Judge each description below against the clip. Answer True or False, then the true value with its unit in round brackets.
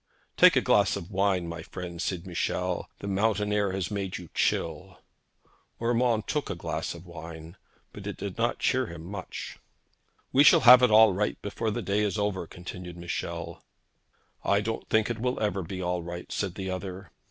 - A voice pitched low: True (95 Hz)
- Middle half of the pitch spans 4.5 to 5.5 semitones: False (3.4 semitones)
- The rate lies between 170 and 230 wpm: True (185 wpm)